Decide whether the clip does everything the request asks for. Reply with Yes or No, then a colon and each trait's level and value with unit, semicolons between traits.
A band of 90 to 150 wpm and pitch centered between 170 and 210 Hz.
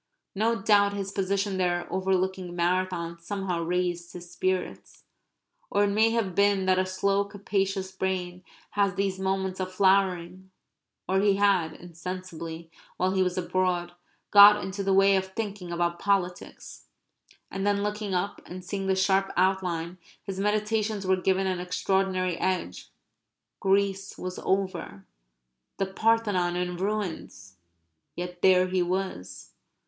Yes: average, 140 wpm; high, 190 Hz